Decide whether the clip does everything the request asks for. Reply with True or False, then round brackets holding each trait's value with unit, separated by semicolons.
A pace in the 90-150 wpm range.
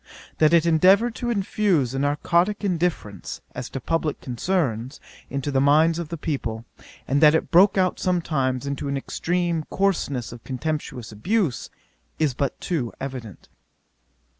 True (145 wpm)